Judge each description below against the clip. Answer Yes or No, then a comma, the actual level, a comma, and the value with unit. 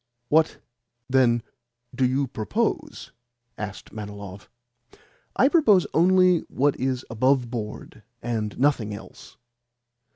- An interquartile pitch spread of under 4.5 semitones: No, average, 5.1 semitones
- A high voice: No, low, 125 Hz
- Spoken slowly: Yes, slow, 100 wpm